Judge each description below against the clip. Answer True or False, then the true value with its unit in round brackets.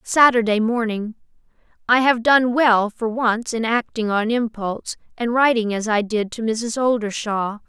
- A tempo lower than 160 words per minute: True (150 wpm)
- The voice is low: False (225 Hz)